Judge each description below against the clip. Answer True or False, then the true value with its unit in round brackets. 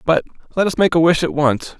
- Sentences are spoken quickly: True (265 wpm)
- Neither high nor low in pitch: True (155 Hz)